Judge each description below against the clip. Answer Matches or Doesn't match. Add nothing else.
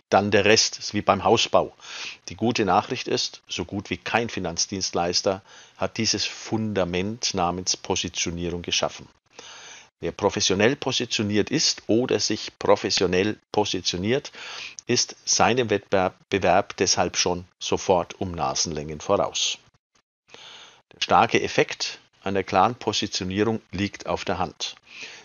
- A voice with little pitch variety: Doesn't match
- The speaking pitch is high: Doesn't match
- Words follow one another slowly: Matches